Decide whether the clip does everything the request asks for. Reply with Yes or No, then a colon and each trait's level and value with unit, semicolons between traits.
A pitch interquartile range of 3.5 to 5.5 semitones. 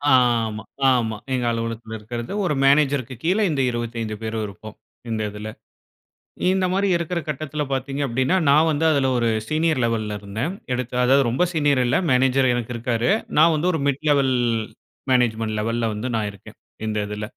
Yes: average, 4.2 semitones